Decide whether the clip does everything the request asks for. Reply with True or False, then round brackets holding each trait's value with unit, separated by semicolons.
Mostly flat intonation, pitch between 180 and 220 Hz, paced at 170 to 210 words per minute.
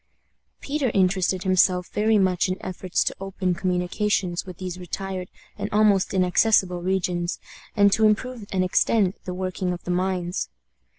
False (1.8 semitones; 185 Hz; 150 wpm)